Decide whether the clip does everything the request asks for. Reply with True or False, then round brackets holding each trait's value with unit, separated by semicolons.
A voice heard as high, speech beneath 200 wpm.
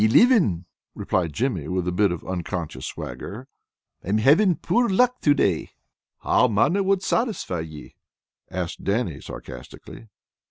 False (105 Hz; 135 wpm)